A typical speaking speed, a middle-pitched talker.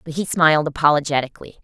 Yes: average, 145 wpm; medium, 150 Hz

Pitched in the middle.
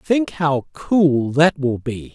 Yes: medium, 145 Hz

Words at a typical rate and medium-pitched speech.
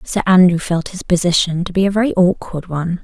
No: fast, 220 wpm; medium, 180 Hz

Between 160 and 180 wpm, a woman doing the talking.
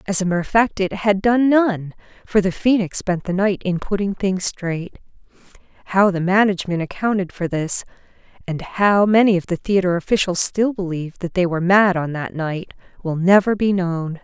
No: average, 190 wpm; female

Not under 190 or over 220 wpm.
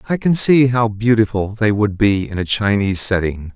Yes: average, 200 wpm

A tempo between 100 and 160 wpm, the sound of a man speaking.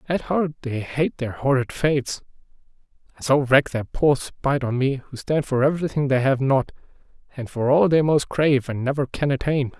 No: average, 195 wpm; male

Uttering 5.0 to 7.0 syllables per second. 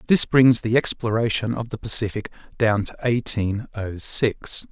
No: 4.5 syllables/s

